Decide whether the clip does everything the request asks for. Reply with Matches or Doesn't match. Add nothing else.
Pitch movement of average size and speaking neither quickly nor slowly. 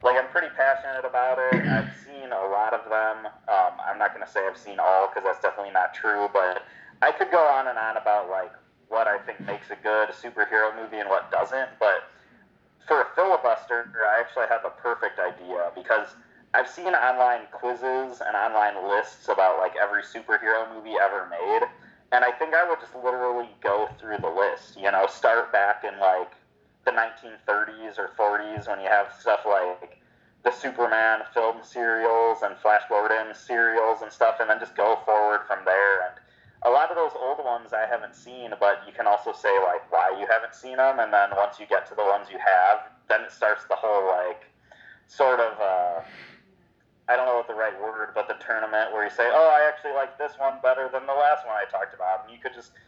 Doesn't match